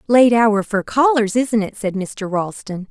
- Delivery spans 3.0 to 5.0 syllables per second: Yes, 4.0 syllables/s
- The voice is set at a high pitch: Yes, high, 215 Hz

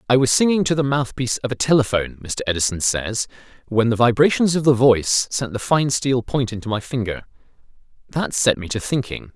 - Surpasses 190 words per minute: Yes, average, 200 wpm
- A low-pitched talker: Yes, low, 125 Hz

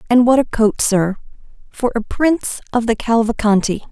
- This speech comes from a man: No, female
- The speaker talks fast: No, average, 170 wpm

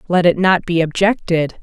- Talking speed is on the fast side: No, average, 185 wpm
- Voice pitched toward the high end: No, medium, 180 Hz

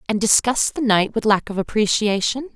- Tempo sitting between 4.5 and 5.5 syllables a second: Yes, 5.2 syllables/s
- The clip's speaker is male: No, female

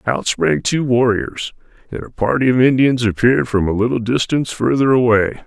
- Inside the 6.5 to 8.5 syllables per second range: No, 5.4 syllables/s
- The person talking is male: Yes, male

